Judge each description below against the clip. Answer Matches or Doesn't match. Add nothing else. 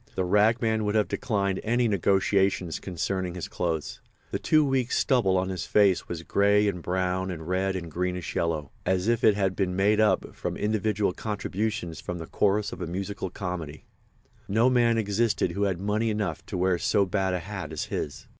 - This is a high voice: Doesn't match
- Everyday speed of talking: Matches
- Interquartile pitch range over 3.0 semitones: Doesn't match